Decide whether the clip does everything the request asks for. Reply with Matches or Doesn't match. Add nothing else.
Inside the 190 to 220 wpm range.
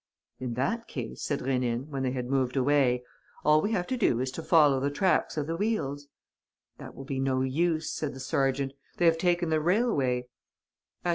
Matches